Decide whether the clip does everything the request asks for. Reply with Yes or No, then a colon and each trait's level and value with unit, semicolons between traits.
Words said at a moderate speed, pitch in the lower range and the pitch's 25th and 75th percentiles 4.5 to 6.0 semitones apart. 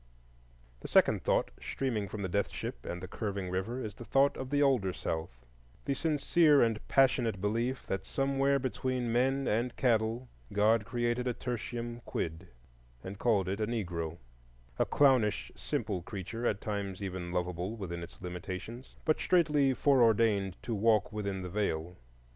Yes: average, 155 wpm; low, 105 Hz; average, 5.1 semitones